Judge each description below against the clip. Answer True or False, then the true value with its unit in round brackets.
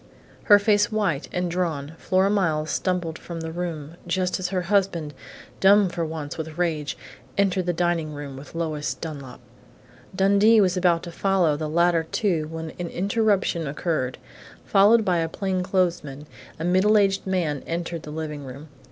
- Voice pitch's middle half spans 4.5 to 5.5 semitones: False (3.4 semitones)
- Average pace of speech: True (160 wpm)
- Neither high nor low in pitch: True (175 Hz)